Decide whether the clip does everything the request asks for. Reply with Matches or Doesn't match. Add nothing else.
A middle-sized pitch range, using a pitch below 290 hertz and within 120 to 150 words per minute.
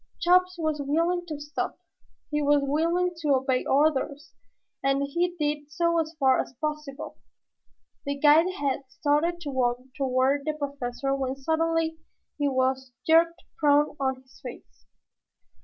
Doesn't match